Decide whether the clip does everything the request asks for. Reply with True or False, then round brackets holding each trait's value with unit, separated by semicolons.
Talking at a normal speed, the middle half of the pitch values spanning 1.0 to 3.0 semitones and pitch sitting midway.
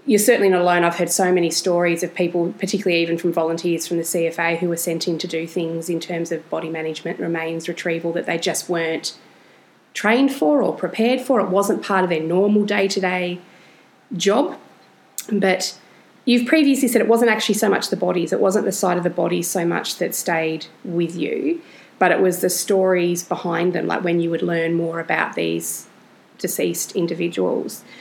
True (195 wpm; 2.5 semitones; 175 Hz)